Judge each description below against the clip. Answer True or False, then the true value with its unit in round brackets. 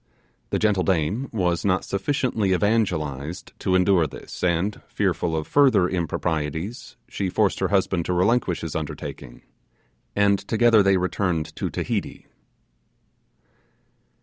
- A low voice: True (95 Hz)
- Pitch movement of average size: True (3.5 semitones)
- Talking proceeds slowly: True (120 wpm)